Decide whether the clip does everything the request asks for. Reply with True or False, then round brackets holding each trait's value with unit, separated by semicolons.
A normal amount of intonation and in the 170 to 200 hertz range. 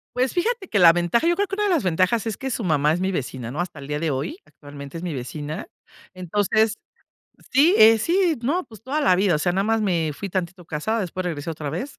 False (7.3 semitones; 185 Hz)